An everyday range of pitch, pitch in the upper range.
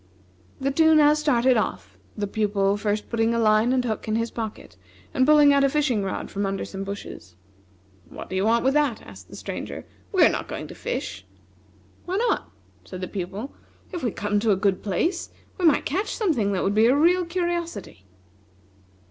No: wide, 6.6 semitones; high, 230 Hz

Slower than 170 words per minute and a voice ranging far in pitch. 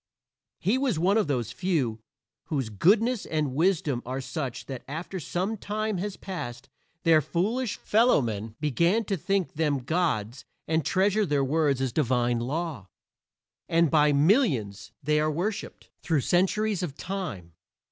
Yes: average, 145 wpm; wide, 6.7 semitones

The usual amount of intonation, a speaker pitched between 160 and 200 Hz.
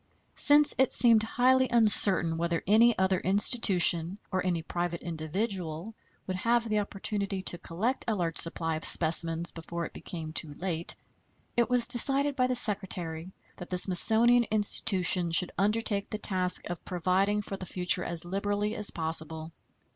Yes: average, 4.2 semitones; high, 190 Hz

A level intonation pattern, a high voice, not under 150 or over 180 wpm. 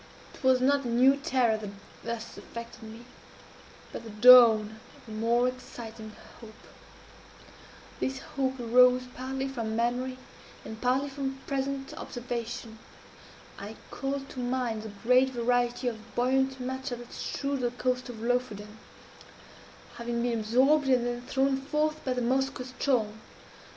No: narrow, 2.3 semitones; very high, 250 Hz; average, 140 wpm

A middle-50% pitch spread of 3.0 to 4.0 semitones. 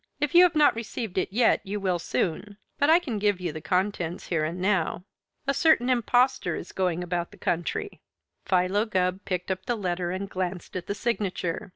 No: average, 4.4 semitones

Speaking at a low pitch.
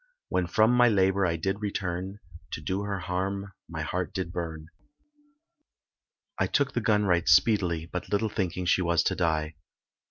Yes: very low, 95 Hz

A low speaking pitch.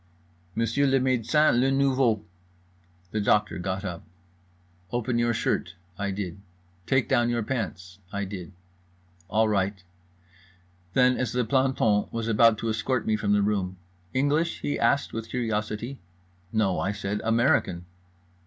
Yes: low, 110 Hz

